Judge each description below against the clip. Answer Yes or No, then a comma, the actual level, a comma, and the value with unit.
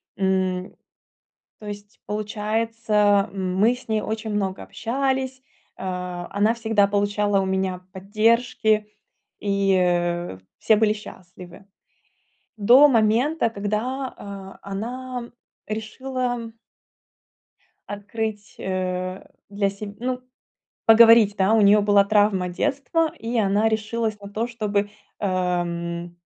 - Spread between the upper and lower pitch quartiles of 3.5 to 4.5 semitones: No, average, 2.8 semitones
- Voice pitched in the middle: No, high, 210 Hz